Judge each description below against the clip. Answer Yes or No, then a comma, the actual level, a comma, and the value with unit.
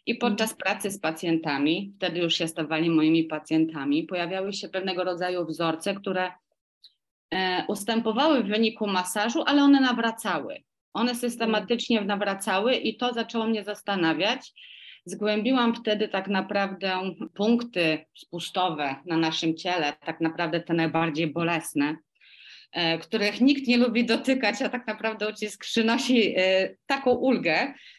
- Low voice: No, high, 200 Hz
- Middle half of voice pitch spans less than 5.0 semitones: No, average, 5.3 semitones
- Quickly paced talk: No, average, 130 wpm